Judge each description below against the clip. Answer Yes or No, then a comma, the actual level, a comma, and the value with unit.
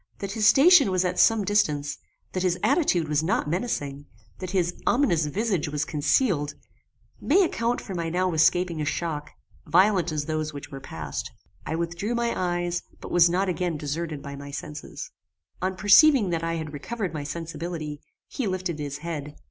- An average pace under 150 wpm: No, average, 175 wpm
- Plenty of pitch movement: No, average, 4.1 semitones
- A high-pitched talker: No, medium, 170 Hz